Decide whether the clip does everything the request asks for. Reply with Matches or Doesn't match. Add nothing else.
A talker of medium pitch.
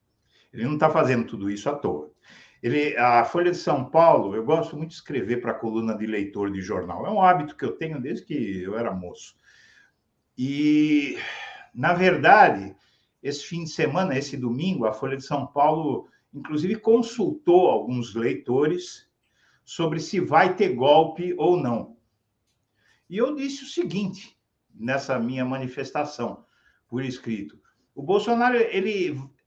Matches